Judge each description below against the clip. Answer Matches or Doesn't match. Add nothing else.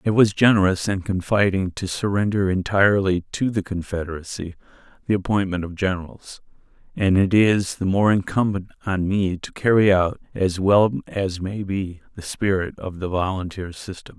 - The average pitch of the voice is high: Doesn't match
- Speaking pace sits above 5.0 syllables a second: Doesn't match